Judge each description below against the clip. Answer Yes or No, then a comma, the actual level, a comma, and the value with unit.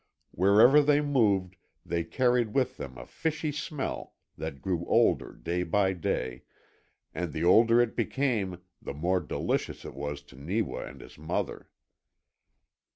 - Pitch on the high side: No, very low, 95 Hz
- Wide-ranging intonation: Yes, wide, 7.5 semitones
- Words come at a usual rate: Yes, average, 145 wpm